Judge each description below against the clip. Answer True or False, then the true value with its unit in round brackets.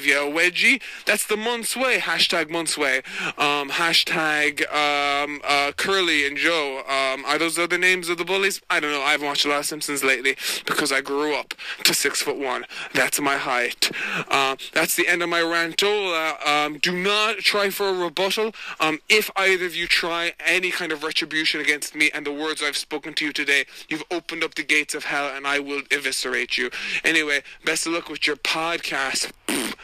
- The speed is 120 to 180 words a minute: False (200 wpm)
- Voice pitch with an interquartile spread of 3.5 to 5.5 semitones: False (3.1 semitones)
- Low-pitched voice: False (155 Hz)